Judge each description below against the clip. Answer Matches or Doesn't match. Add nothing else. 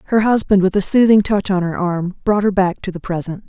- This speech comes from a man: Doesn't match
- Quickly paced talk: Matches